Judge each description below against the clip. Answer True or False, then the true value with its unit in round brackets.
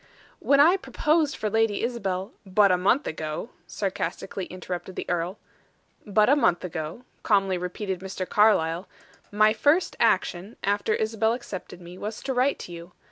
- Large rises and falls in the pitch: False (3.7 semitones)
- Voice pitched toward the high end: True (200 Hz)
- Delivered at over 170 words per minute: False (160 wpm)